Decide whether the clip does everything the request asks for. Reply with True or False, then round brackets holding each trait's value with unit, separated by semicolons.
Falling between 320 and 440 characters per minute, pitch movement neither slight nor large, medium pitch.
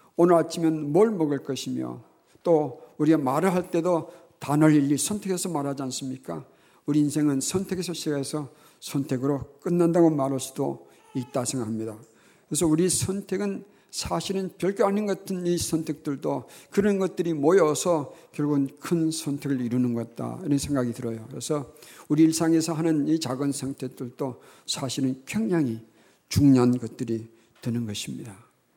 True (330 characters per minute; 4.4 semitones; 150 Hz)